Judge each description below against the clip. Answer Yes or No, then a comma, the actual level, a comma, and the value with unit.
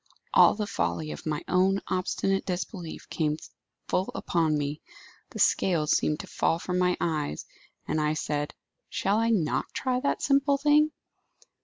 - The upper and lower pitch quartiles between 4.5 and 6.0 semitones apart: Yes, average, 5.1 semitones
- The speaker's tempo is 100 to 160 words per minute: Yes, average, 155 wpm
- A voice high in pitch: No, medium, 180 Hz